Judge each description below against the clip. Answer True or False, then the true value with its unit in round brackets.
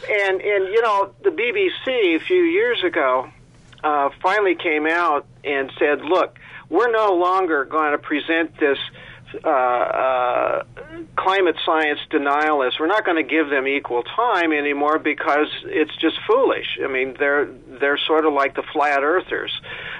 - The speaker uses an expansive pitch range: True (6.6 semitones)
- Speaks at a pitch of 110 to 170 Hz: True (155 Hz)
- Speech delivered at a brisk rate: False (155 wpm)